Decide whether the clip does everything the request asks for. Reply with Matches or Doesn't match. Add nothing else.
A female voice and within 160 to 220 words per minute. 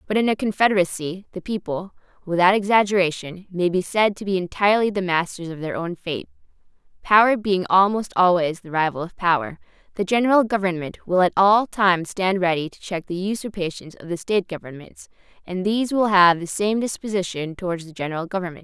Matches